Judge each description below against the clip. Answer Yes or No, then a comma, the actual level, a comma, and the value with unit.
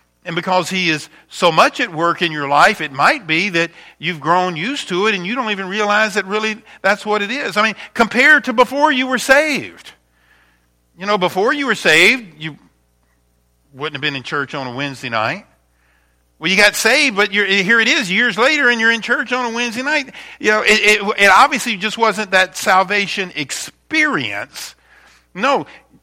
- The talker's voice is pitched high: Yes, high, 200 Hz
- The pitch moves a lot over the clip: Yes, wide, 7.0 semitones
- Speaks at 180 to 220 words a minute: Yes, average, 200 wpm